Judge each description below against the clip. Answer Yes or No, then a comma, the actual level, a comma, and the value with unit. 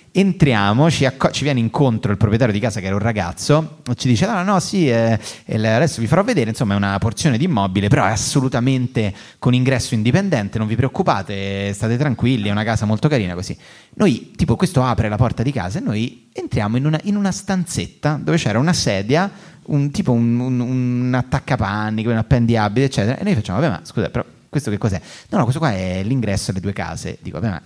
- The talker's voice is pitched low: Yes, low, 120 Hz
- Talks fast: Yes, fast, 215 wpm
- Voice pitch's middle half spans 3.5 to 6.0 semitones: Yes, average, 5.0 semitones